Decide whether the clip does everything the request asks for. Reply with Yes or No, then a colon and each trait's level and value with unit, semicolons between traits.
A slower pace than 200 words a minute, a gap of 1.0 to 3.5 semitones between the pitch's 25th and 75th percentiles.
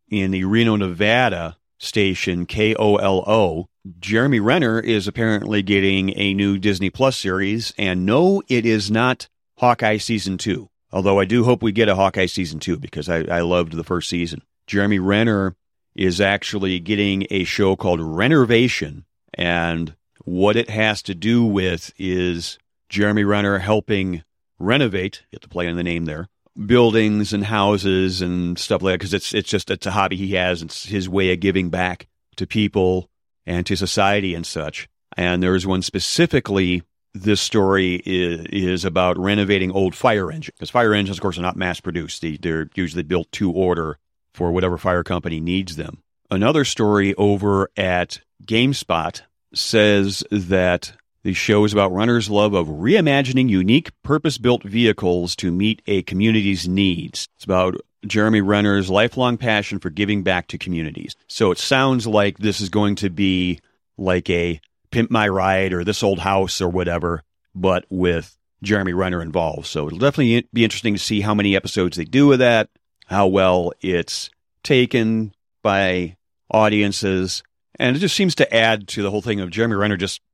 Yes: average, 170 wpm; average, 2.8 semitones